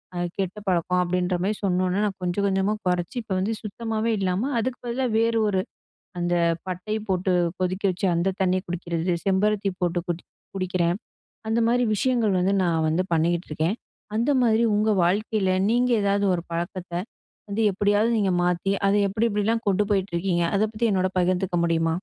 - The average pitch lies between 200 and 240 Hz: No, high, 190 Hz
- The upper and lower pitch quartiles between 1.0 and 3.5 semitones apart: Yes, average, 3.0 semitones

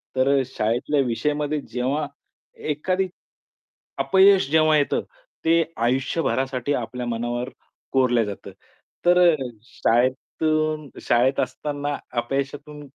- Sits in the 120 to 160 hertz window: Yes, medium, 140 Hz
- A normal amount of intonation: Yes, average, 3.6 semitones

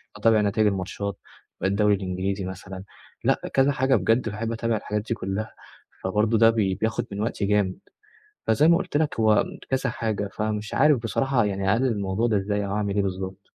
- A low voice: Yes, low, 105 Hz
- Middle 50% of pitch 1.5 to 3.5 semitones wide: Yes, narrow, 2.6 semitones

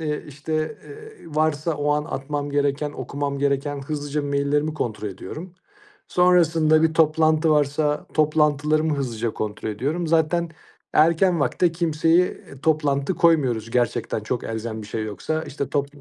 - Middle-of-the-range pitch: Yes, medium, 150 Hz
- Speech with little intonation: Yes, narrow, 2.3 semitones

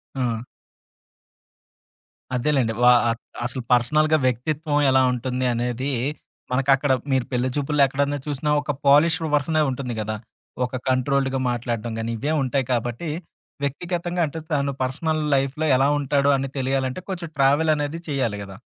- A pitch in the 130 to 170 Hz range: Yes, low, 135 Hz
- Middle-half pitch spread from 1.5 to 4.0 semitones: Yes, average, 2.8 semitones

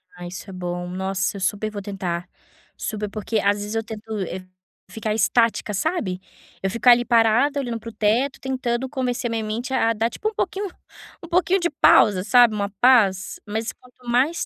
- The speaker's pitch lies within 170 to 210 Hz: No, high, 220 Hz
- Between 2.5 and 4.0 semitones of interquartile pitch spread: Yes, average, 3.7 semitones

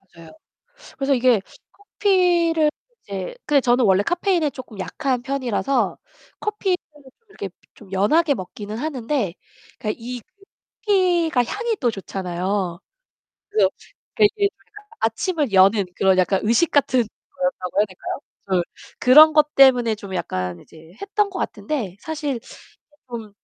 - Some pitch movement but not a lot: No, wide, 8.0 semitones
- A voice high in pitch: Yes, very high, 250 Hz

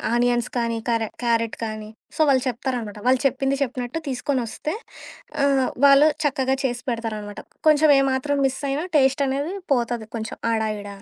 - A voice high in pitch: Yes, very high, 255 Hz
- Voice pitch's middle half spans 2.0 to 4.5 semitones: Yes, average, 2.8 semitones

